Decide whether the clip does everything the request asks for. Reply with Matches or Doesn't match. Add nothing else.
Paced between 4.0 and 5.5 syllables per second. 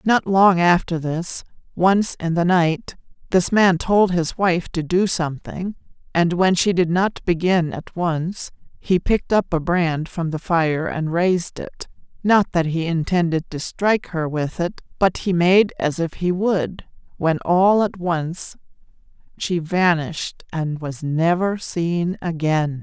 Doesn't match